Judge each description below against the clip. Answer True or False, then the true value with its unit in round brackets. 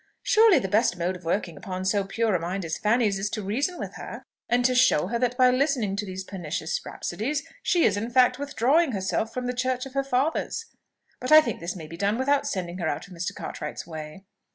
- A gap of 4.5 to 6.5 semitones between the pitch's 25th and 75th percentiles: True (5.5 semitones)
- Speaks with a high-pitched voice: True (220 Hz)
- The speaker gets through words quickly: True (230 wpm)